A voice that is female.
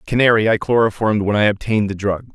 No: male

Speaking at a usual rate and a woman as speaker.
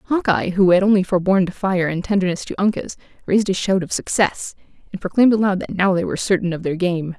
No: fast, 225 wpm; female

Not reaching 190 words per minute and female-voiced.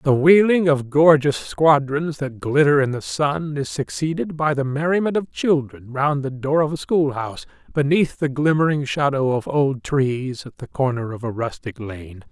No: average, 180 wpm; male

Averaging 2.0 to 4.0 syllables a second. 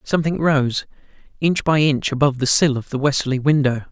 No: 5.9 syllables/s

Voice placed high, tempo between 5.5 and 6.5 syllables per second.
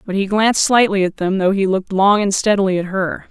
Yes: high, 195 Hz; 5.9 syllables/s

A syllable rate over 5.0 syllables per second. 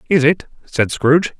No: 4.9 syllables/s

